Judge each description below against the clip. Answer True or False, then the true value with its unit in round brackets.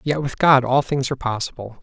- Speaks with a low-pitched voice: True (130 Hz)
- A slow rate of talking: False (230 wpm)